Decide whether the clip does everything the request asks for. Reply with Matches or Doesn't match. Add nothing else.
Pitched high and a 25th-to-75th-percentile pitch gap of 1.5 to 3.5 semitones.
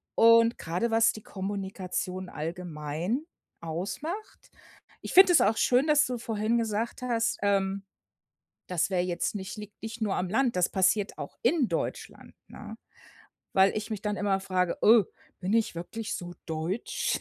Doesn't match